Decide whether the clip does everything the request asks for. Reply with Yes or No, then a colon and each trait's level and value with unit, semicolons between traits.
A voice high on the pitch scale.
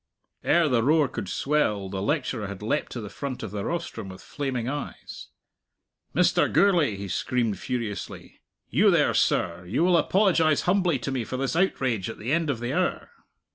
No: low, 130 Hz